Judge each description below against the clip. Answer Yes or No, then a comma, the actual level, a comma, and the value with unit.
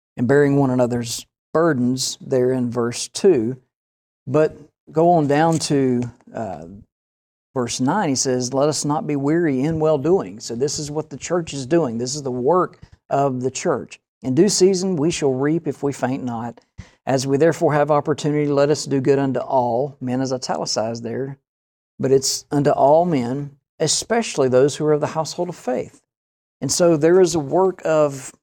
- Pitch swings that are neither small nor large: Yes, average, 3.5 semitones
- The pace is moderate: Yes, average, 185 wpm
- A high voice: No, medium, 140 Hz